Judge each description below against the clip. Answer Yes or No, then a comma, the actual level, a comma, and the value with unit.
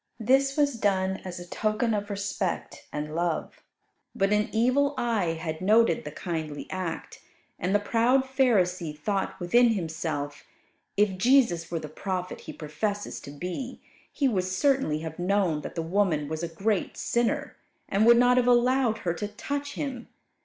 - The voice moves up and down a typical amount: No, wide, 5.7 semitones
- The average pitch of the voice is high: Yes, high, 200 Hz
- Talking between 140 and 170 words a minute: Yes, average, 165 wpm